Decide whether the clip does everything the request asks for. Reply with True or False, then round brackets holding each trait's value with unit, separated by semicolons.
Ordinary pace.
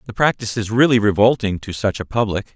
False (210 wpm)